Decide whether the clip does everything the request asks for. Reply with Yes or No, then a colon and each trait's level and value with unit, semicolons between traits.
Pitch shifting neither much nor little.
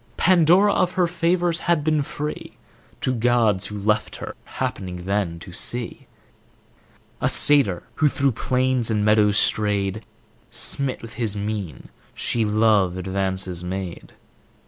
No: wide, 6.3 semitones